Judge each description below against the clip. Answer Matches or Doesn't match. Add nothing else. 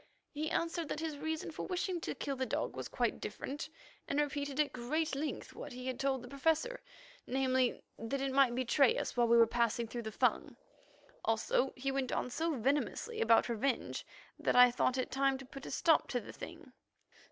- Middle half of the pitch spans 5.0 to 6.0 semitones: Doesn't match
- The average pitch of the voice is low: Doesn't match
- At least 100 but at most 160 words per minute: Doesn't match